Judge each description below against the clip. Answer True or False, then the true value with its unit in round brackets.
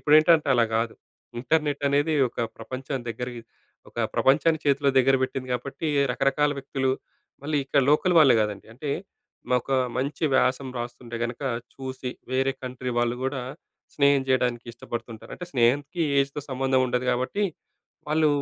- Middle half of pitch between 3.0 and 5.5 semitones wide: False (2.6 semitones)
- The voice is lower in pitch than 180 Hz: True (135 Hz)